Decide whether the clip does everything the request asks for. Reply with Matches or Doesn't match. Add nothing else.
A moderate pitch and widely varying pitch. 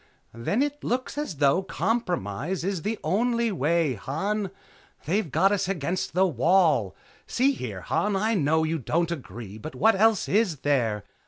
Matches